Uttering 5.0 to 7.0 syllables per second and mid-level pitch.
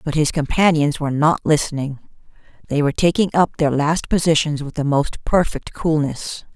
Yes: 5.2 syllables/s; medium, 150 Hz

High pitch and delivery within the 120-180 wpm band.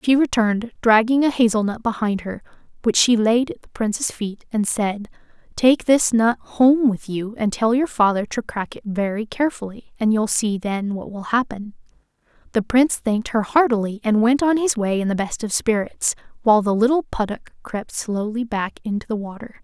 No: high, 225 Hz; average, 195 wpm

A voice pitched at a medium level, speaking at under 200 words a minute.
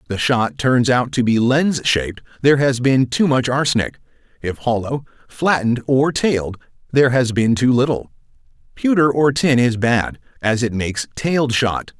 No: low, 125 Hz; average, 175 wpm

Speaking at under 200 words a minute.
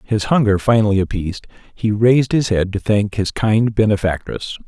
Yes: average, 165 wpm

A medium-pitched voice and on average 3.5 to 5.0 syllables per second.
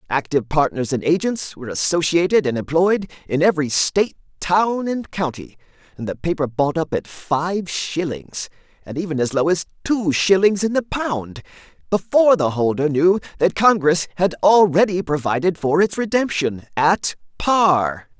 Yes: medium, 165 Hz; 4.7 syllables/s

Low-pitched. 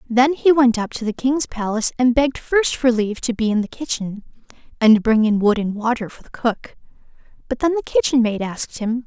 No: high, 235 Hz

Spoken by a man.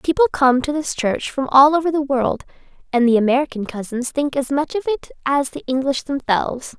No: female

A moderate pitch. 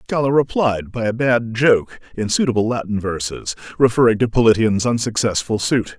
No: low, 115 Hz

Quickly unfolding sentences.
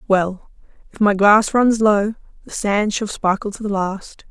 No: average, 180 wpm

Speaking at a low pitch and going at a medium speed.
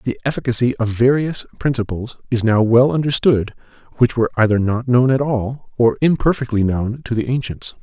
Yes: low, 120 Hz; average, 170 wpm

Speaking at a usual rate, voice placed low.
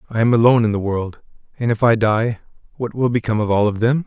No: fast, 250 wpm; low, 115 Hz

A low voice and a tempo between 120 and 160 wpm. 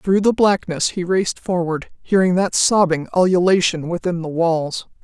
No: medium, 180 Hz; average, 155 wpm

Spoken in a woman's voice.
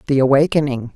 Yes: female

